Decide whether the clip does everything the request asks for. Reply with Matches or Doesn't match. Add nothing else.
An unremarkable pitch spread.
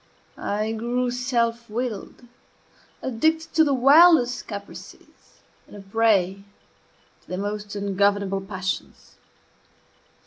Matches